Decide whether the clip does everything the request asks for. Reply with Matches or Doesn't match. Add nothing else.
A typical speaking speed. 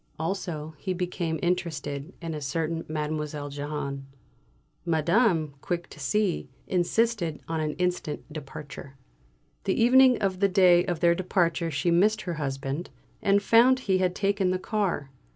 Matches